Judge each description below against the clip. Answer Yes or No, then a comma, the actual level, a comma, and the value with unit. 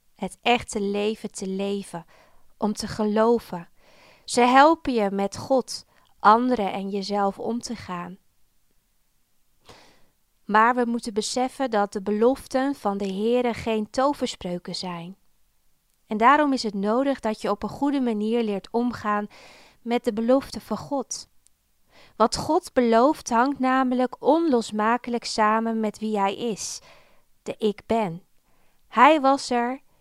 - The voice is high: Yes, high, 225 Hz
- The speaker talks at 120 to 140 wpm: Yes, slow, 135 wpm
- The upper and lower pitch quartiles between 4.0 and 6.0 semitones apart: No, average, 3.5 semitones